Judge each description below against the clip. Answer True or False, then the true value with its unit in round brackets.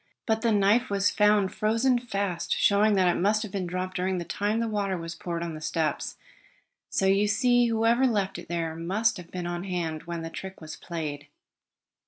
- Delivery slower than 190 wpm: False (205 wpm)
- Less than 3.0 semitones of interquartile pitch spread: False (3.8 semitones)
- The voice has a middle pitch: False (195 Hz)